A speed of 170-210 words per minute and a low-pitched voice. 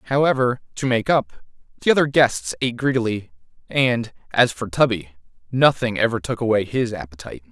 No: average, 150 wpm; low, 125 Hz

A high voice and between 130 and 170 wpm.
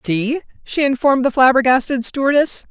Yes: very high, 260 Hz; slow, 135 wpm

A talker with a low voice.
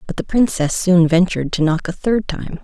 No: medium, 175 Hz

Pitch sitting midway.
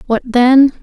No: very high, 250 Hz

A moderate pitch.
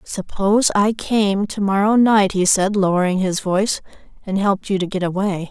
No: high, 195 Hz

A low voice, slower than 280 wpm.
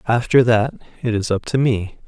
Yes: low, 115 Hz; fast, 205 wpm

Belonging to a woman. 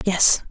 Yes: female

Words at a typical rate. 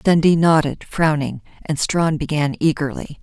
No: slow, 130 wpm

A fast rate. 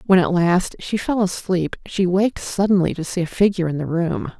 Yes: fast, 220 wpm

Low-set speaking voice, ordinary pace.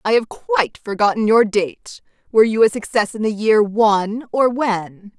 No: high, 215 Hz; average, 185 wpm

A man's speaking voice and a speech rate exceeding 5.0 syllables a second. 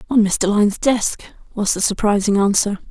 No: female; 5.3 syllables/s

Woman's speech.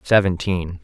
No: male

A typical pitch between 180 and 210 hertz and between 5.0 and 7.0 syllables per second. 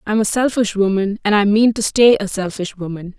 Yes: high, 205 Hz; 5.3 syllables/s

